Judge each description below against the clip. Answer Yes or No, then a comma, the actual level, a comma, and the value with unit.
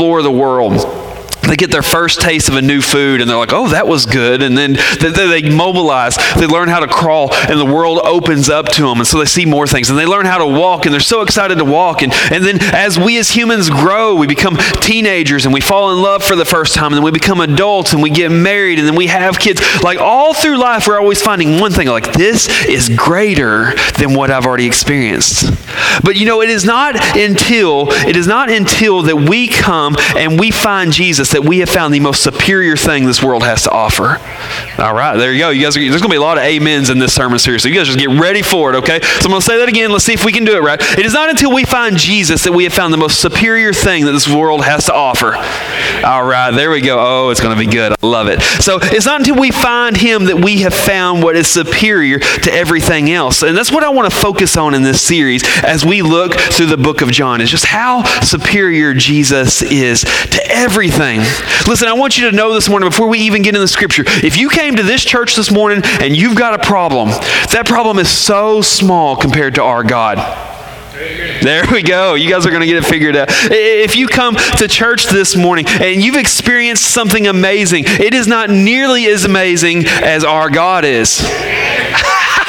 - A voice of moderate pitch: Yes, medium, 175 Hz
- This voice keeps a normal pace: No, fast, 240 wpm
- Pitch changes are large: Yes, wide, 5.9 semitones